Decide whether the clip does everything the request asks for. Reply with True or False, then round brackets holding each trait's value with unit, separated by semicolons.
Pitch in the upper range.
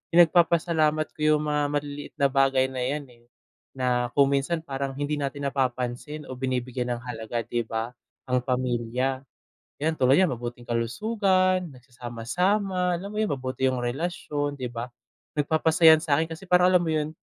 False (140 Hz)